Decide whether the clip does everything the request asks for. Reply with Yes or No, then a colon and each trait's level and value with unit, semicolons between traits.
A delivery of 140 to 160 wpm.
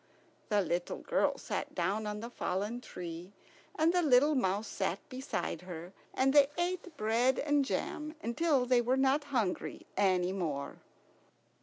Yes: average, 150 wpm